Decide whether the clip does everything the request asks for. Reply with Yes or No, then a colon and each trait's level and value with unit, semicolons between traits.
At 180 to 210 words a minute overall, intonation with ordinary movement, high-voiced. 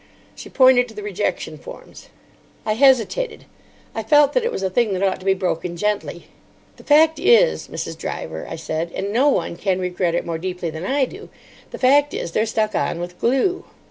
No: average, 200 wpm; wide, 8.0 semitones; high, 220 Hz